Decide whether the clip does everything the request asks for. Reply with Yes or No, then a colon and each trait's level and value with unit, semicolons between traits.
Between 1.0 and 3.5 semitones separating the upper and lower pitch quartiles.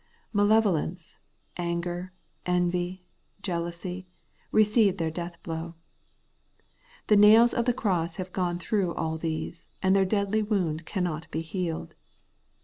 Yes: average, 3.0 semitones